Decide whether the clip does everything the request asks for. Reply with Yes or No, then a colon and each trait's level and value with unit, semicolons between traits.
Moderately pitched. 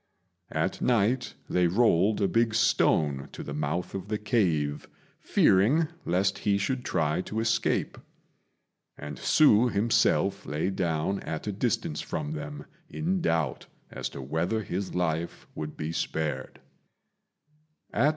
No: very low, 95 Hz